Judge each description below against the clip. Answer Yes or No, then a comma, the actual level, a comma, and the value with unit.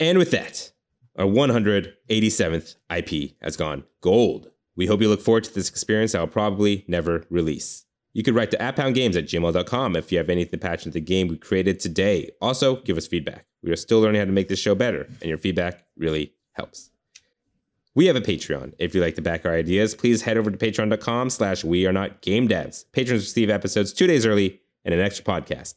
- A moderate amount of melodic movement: Yes, average, 4.2 semitones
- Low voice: Yes, very low, 95 Hz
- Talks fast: Yes, fast, 210 wpm